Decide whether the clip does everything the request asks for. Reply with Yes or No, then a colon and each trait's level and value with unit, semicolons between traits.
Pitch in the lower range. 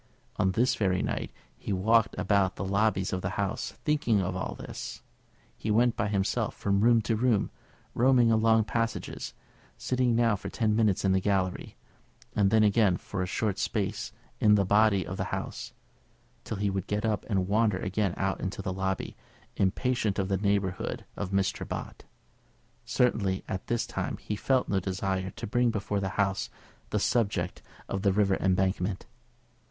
Yes: low, 100 Hz